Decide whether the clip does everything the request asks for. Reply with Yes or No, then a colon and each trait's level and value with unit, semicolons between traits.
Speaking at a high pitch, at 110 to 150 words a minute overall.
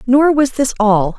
No: very high, 255 Hz; fast, 205 wpm